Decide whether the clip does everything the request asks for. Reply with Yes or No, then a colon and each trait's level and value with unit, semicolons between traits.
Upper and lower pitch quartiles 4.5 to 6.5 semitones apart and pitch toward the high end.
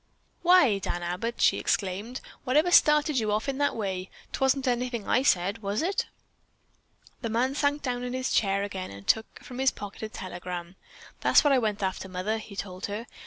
Yes: average, 5.2 semitones; high, 220 Hz